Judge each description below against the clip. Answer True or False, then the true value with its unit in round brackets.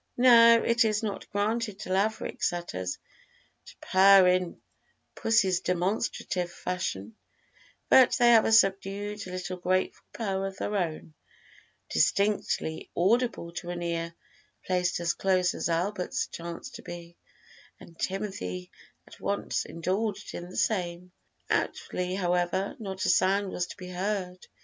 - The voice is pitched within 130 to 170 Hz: False (185 Hz)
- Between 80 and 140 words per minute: True (135 wpm)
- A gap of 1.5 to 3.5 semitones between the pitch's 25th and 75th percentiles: True (2.8 semitones)